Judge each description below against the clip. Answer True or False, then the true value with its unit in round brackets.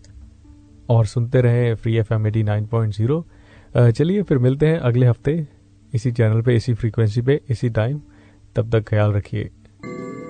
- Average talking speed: True (145 wpm)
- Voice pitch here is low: True (115 Hz)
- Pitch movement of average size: True (3.1 semitones)